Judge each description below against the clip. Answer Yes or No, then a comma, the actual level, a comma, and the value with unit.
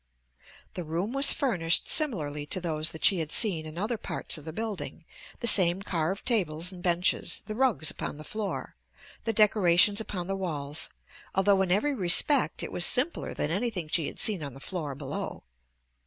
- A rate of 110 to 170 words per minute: No, average, 185 wpm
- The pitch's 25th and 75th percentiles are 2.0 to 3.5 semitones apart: No, average, 5.1 semitones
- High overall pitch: No, medium, 180 Hz